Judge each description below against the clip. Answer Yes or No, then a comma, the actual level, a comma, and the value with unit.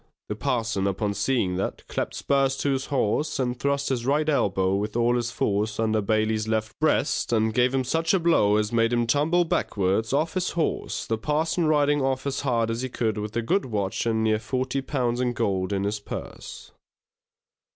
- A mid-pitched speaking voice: No, low, 120 Hz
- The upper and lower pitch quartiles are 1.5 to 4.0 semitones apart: No, average, 4.4 semitones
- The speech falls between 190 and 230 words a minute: Yes, average, 200 wpm